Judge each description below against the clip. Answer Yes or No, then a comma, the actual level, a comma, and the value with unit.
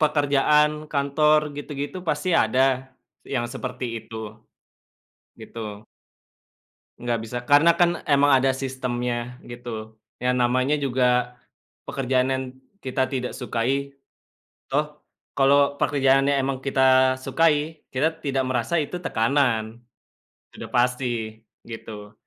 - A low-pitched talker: Yes, low, 130 Hz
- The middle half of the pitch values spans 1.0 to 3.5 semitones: Yes, average, 2.8 semitones